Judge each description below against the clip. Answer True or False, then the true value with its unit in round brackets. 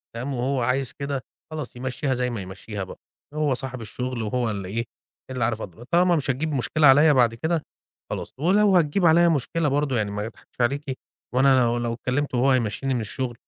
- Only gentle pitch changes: False (3.6 semitones)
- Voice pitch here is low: True (130 Hz)